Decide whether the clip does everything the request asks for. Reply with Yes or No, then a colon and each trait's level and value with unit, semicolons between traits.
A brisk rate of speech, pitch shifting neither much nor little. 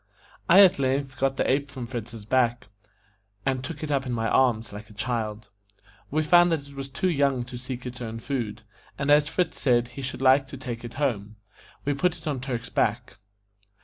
Yes: fast, 210 wpm; average, 3.0 semitones